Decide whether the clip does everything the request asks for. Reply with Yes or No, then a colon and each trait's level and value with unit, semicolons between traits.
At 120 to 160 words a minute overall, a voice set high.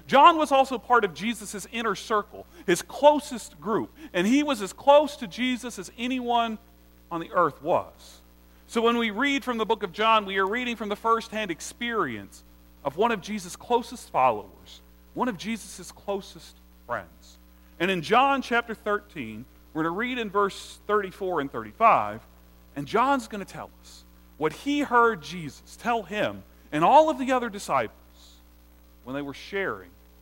No: average, 175 wpm; high, 205 Hz